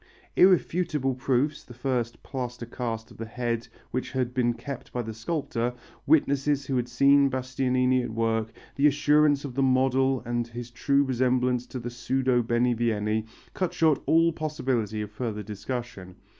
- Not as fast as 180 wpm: Yes, average, 155 wpm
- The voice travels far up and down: No, narrow, 2.6 semitones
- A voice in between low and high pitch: No, low, 125 Hz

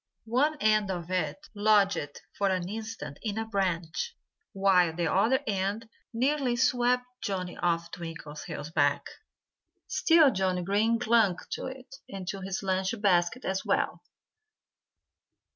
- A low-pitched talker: No, high, 195 Hz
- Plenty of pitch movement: No, average, 4.3 semitones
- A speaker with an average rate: No, slow, 130 wpm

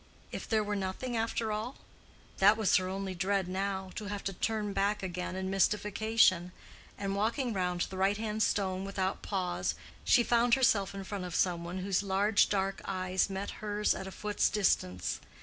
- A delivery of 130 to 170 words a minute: No, average, 180 wpm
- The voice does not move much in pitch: Yes, narrow, 1.9 semitones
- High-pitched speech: Yes, high, 195 Hz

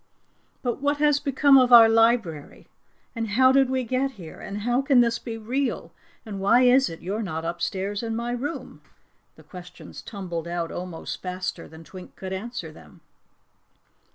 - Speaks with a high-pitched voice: Yes, high, 225 Hz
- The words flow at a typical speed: Yes, average, 170 wpm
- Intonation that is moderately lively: No, wide, 5.8 semitones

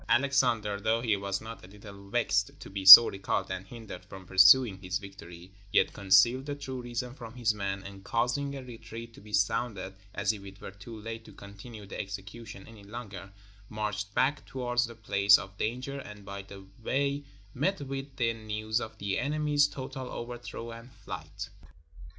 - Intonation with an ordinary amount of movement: Yes, average, 3.7 semitones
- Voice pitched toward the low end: Yes, low, 110 Hz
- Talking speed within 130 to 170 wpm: No, average, 180 wpm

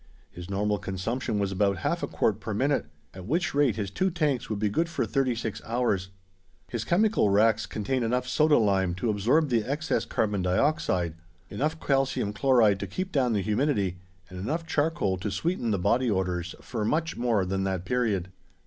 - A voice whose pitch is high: No, low, 110 Hz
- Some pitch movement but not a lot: No, wide, 5.9 semitones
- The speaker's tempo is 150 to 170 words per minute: No, average, 185 wpm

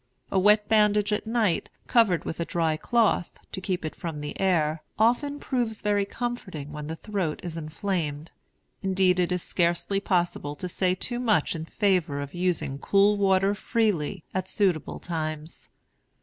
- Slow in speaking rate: No, average, 165 wpm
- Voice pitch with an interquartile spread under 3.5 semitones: No, average, 4.4 semitones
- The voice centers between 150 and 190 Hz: Yes, medium, 185 Hz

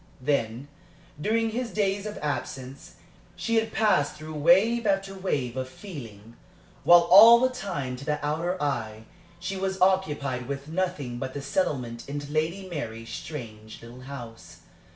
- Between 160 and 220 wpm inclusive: No, average, 150 wpm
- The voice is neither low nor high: Yes, medium, 150 Hz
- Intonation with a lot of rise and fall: Yes, wide, 7.1 semitones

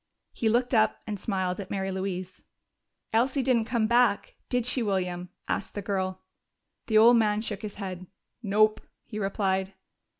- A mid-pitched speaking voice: No, high, 210 Hz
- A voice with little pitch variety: No, average, 3.1 semitones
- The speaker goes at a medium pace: Yes, average, 160 wpm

